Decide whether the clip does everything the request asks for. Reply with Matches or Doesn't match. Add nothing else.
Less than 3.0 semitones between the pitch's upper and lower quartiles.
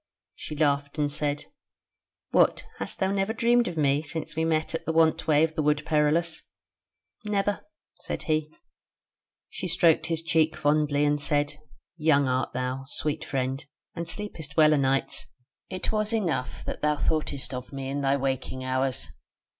Matches